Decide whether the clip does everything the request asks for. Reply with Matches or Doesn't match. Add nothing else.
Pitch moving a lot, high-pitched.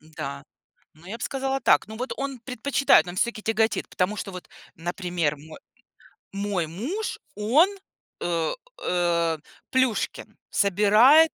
Matches